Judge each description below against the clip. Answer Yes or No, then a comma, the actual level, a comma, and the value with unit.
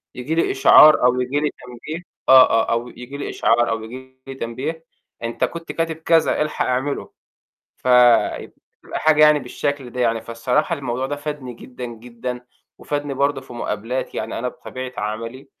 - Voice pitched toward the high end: No, low, 130 Hz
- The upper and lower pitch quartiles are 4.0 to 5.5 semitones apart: No, average, 3.3 semitones